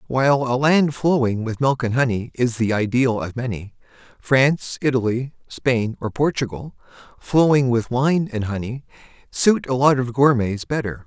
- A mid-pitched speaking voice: No, low, 125 Hz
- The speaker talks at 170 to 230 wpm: No, average, 155 wpm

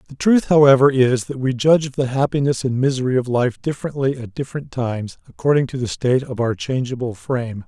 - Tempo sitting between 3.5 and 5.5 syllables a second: No, 6.1 syllables/s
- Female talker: No, male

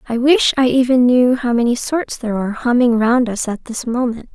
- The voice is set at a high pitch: Yes, high, 245 Hz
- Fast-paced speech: Yes, fast, 220 wpm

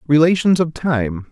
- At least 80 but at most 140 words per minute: Yes, slow, 135 wpm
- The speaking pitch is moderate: Yes, medium, 150 Hz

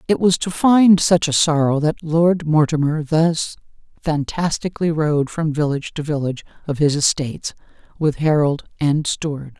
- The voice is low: No, medium, 155 Hz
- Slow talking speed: No, average, 150 wpm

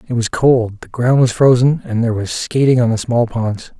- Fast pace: Yes, fast, 235 wpm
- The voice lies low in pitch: Yes, low, 120 Hz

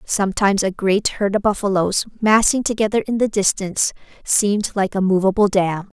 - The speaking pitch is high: Yes, high, 200 Hz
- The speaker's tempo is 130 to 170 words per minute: Yes, average, 160 wpm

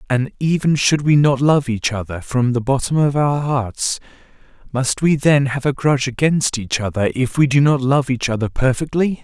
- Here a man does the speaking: Yes, male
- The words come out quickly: No, average, 195 wpm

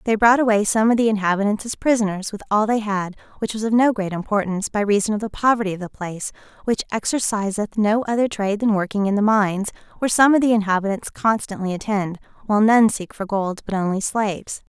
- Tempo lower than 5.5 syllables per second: No, 6.3 syllables/s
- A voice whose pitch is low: No, high, 210 Hz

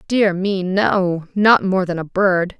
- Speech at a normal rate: Yes, average, 185 wpm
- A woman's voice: Yes, female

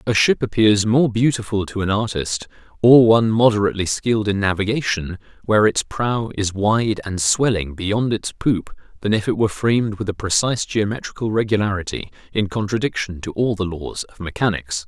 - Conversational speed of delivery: Yes, average, 170 wpm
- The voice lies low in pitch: Yes, low, 105 Hz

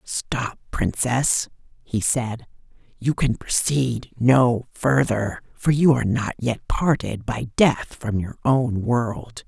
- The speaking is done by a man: No, female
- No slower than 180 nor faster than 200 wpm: No, slow, 135 wpm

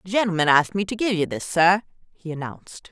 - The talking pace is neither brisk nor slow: No, fast, 225 wpm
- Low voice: No, medium, 185 Hz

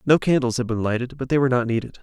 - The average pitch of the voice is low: Yes, low, 125 Hz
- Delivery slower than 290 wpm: No, fast, 295 wpm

